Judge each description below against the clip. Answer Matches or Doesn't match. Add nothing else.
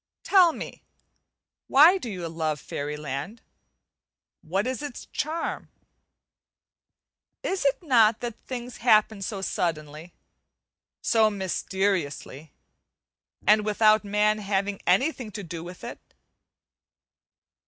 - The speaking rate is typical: Doesn't match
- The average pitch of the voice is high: Matches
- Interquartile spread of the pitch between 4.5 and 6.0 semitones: Matches